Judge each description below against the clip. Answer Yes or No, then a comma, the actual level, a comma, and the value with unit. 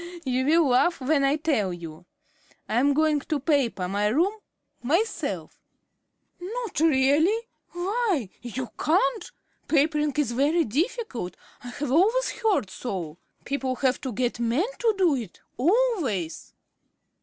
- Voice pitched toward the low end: No, very high, 285 Hz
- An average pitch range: No, wide, 6.2 semitones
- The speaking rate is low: Yes, slow, 130 wpm